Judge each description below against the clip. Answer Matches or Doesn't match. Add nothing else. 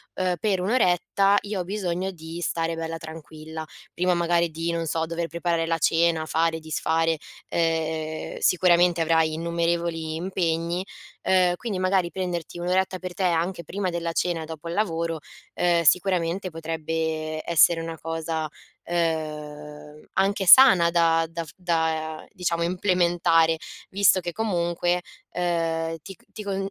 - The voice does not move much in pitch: Matches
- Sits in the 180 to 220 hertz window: Doesn't match